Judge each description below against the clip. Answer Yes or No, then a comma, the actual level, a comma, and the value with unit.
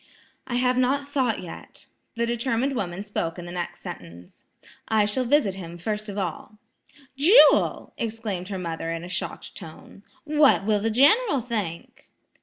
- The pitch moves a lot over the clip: Yes, wide, 6.1 semitones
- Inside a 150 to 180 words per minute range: Yes, average, 160 wpm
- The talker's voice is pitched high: Yes, high, 215 Hz